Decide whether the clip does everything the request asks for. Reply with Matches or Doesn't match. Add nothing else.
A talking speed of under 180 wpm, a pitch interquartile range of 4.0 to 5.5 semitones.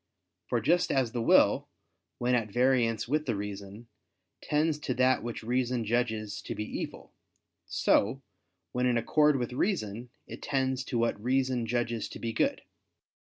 Doesn't match